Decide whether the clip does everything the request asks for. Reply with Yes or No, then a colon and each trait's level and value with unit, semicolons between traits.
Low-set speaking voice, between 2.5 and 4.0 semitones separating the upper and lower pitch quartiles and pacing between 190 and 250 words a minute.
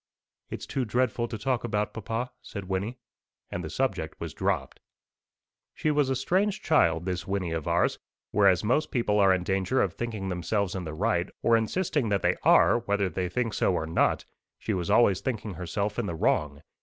No: low, 105 Hz; average, 4.7 semitones; average, 195 wpm